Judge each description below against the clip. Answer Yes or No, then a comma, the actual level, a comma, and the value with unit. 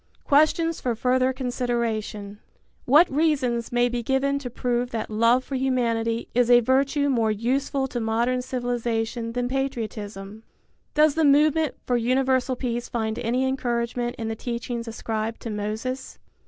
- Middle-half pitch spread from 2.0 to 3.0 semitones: Yes, narrow, 2.4 semitones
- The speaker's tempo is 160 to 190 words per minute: No, average, 145 wpm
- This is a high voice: Yes, high, 245 Hz